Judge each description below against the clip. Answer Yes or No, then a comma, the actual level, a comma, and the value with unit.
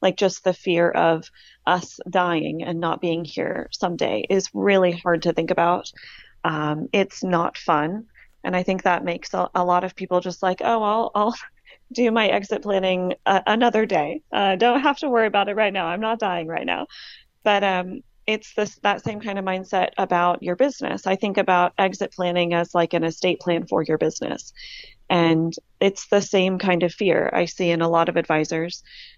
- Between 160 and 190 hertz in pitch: Yes, medium, 185 Hz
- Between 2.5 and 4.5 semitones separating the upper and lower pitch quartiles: Yes, average, 3.0 semitones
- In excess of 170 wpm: Yes, average, 200 wpm